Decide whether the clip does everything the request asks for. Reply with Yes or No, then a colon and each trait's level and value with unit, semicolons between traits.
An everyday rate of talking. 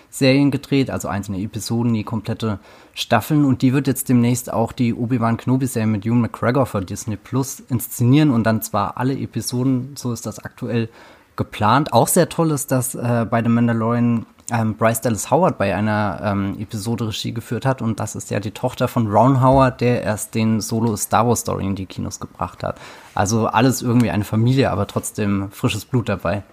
No: fast, 195 wpm